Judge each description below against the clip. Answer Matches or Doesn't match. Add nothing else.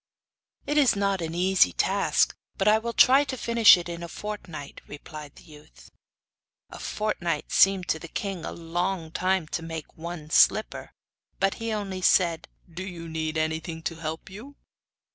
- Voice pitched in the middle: Matches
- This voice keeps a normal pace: Matches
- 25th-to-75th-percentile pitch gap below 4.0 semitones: Matches